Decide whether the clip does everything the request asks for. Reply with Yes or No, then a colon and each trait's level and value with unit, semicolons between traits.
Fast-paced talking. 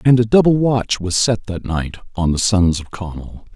Yes: fast, 220 wpm